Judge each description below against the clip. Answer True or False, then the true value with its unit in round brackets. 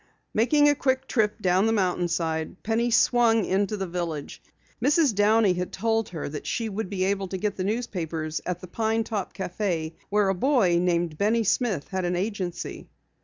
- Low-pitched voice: False (195 Hz)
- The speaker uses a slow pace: False (180 wpm)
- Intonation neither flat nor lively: True (4.0 semitones)